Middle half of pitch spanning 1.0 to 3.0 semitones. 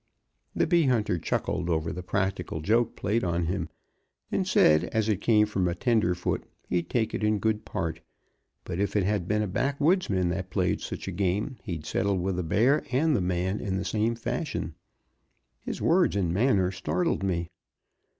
No: average, 4.1 semitones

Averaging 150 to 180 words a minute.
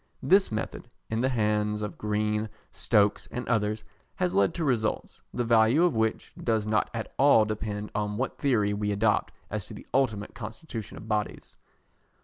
Yes: average, 170 wpm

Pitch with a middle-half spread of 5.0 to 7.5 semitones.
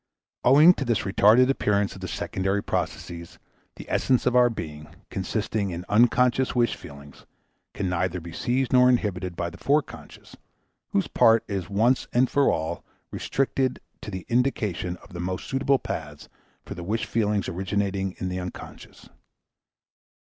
Yes: wide, 5.6 semitones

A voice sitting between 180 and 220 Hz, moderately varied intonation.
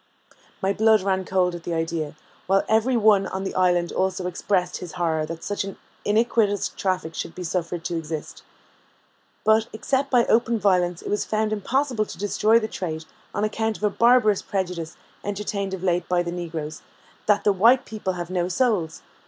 Yes: high, 190 Hz; average, 3.6 semitones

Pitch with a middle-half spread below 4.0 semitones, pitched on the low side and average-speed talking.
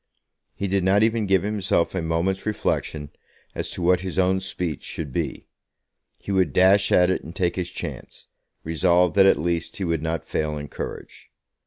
Yes: average, 2.7 semitones; very low, 90 Hz; average, 185 wpm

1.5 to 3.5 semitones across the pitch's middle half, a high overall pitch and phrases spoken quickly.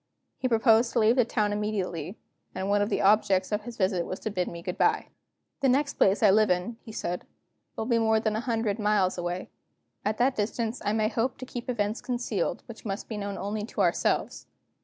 Yes: average, 2.8 semitones; high, 215 Hz; fast, 220 wpm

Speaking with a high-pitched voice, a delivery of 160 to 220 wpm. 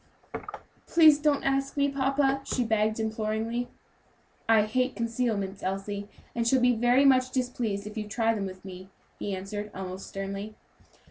No: high, 225 Hz; average, 150 wpm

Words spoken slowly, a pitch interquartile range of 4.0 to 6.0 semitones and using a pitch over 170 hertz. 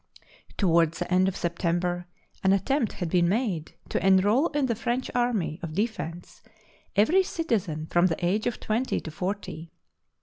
No: average, 165 wpm; average, 5.0 semitones; high, 190 Hz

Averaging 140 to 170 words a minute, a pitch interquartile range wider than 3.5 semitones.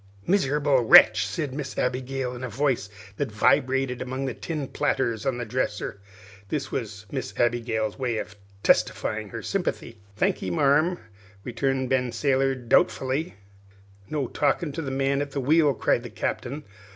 No: average, 150 wpm; average, 2.8 semitones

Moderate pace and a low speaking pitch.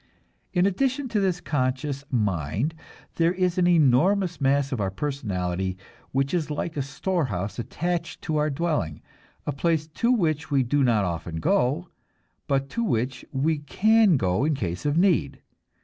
No: average, 160 wpm; medium, 145 Hz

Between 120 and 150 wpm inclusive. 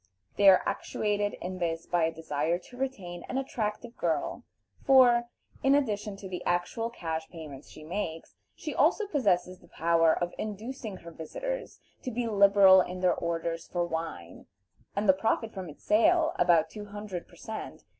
No: average, 170 wpm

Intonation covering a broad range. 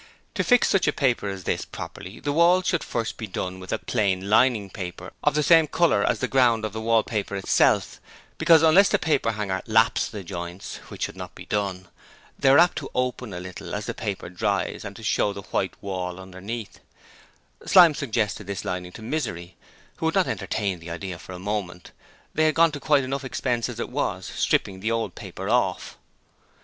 Yes: wide, 6.0 semitones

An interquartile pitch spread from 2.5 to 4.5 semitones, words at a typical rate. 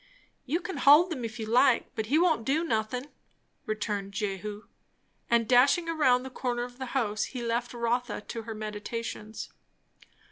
Yes: average, 3.6 semitones; average, 165 wpm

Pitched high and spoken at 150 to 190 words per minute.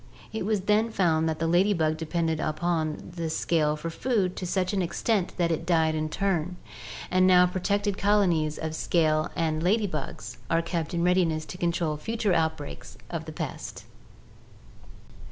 No: medium, 170 Hz; average, 170 wpm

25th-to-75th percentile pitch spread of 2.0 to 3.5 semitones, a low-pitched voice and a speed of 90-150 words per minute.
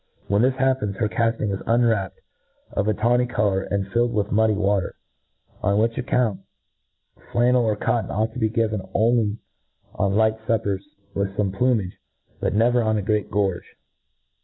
No: average, 2.8 semitones; low, 110 Hz; average, 165 wpm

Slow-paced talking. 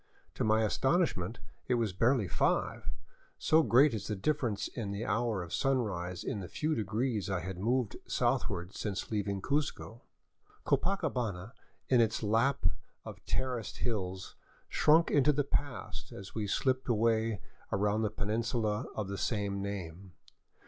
No: average, 150 wpm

